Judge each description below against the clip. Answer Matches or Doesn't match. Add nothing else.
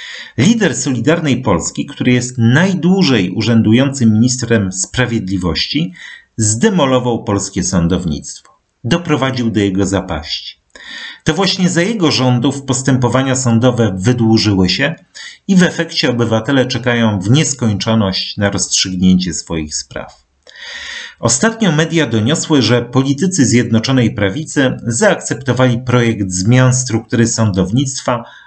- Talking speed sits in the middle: Doesn't match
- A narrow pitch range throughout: Doesn't match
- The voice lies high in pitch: Doesn't match